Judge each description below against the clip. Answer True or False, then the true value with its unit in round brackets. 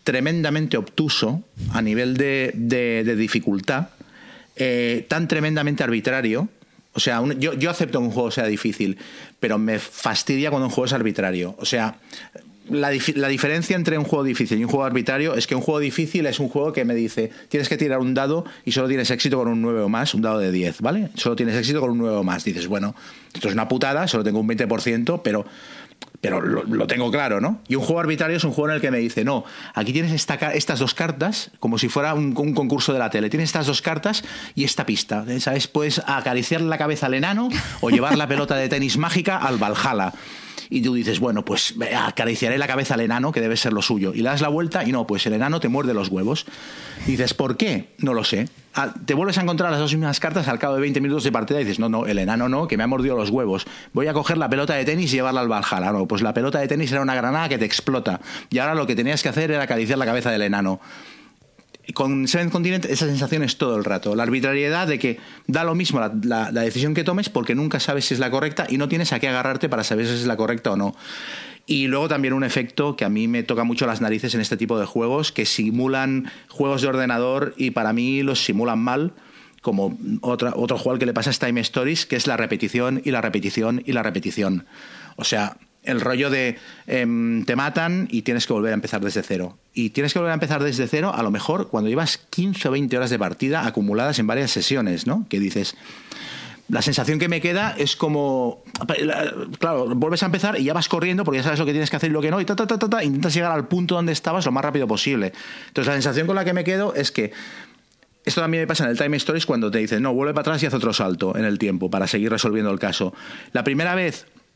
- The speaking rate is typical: False (245 wpm)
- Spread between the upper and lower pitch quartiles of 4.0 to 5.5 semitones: True (5.2 semitones)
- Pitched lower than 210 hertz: True (135 Hz)